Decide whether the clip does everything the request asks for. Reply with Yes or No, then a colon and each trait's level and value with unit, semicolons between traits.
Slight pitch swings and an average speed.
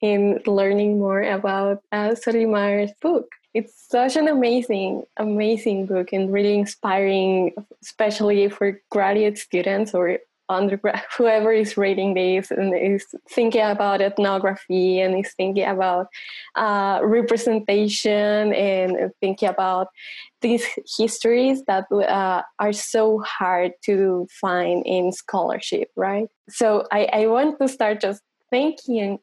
No: narrow, 2.3 semitones; slow, 125 wpm